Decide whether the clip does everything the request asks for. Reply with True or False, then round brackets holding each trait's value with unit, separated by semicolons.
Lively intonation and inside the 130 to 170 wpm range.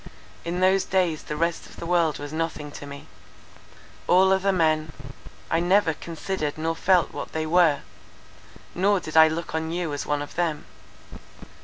False (2.5 semitones; 165 wpm)